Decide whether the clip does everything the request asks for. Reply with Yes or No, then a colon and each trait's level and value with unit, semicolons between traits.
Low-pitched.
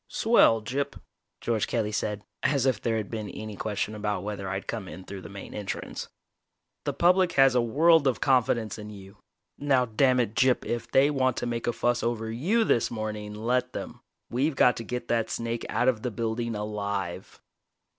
Yes: low, 115 Hz